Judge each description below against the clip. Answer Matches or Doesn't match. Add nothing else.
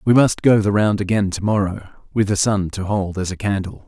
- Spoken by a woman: Doesn't match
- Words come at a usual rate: Doesn't match